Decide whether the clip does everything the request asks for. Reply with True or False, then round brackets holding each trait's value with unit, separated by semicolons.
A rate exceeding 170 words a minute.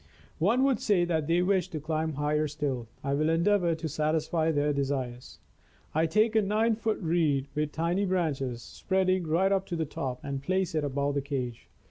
True (190 wpm)